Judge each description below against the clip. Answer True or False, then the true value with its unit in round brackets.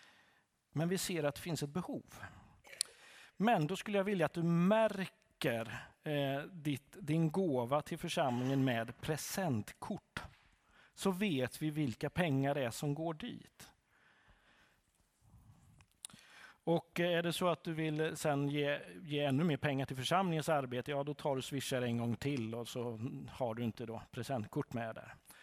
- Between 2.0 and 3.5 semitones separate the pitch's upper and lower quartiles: False (4.6 semitones)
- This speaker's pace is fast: False (155 wpm)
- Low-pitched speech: False (145 Hz)